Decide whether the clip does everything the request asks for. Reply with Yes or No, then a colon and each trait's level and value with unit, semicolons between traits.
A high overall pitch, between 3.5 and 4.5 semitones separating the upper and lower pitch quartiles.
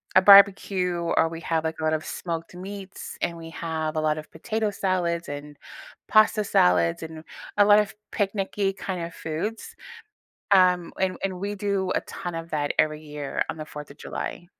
No: medium, 170 Hz; average, 3.8 semitones